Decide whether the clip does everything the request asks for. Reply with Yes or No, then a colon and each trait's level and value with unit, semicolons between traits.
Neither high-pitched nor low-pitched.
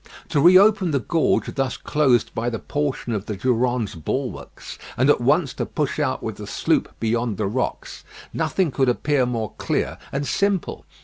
No: low, 130 Hz